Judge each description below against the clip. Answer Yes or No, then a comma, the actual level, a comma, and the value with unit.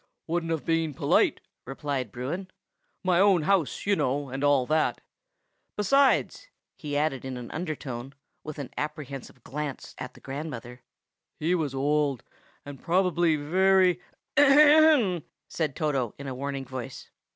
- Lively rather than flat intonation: No, average, 4.7 semitones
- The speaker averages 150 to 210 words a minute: No, average, 140 wpm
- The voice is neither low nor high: Yes, medium, 150 Hz